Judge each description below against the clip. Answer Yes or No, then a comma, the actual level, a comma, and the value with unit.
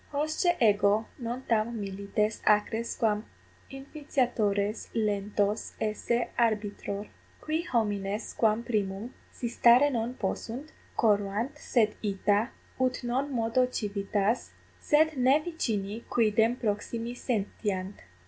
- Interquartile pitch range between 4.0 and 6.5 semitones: No, average, 3.2 semitones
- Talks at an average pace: No, slow, 105 wpm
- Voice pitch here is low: No, high, 225 Hz